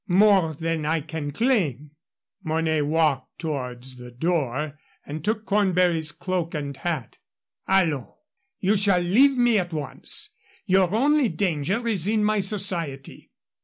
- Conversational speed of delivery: No, slow, 130 wpm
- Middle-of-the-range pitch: Yes, medium, 170 Hz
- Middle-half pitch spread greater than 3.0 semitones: Yes, average, 5.0 semitones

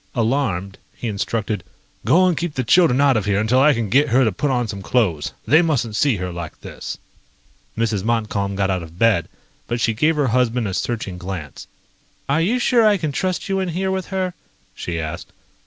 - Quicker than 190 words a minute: Yes, fast, 205 wpm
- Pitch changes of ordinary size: No, wide, 7.3 semitones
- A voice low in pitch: Yes, low, 115 Hz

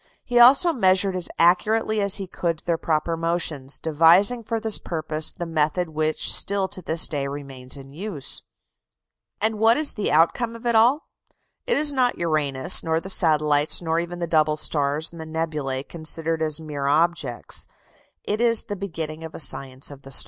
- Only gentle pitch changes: No, average, 4.8 semitones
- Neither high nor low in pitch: Yes, medium, 165 Hz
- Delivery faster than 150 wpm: Yes, average, 185 wpm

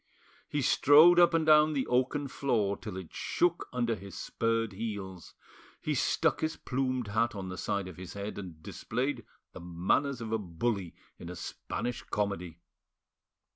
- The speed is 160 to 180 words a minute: Yes, average, 165 wpm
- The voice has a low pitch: Yes, low, 115 Hz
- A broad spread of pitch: Yes, wide, 5.9 semitones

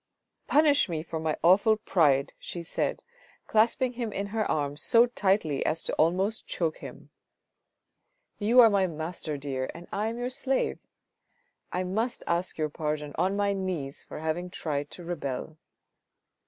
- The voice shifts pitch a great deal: Yes, wide, 5.8 semitones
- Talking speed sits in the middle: Yes, average, 170 wpm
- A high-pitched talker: No, medium, 180 Hz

